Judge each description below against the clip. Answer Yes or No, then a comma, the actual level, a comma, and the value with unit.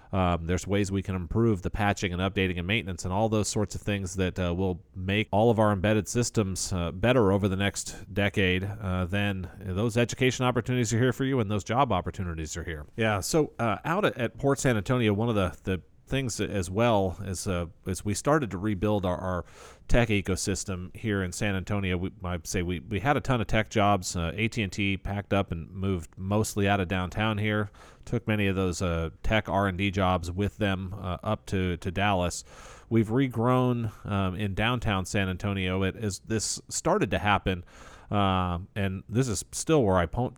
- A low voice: Yes, low, 100 Hz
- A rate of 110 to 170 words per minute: No, fast, 205 wpm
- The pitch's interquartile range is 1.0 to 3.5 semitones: Yes, average, 2.9 semitones